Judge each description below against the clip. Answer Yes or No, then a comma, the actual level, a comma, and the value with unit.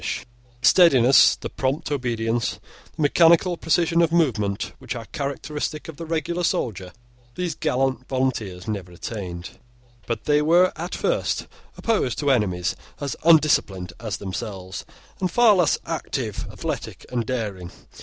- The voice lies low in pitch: Yes, low, 130 Hz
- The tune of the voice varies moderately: No, wide, 7.4 semitones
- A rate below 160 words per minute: Yes, slow, 135 wpm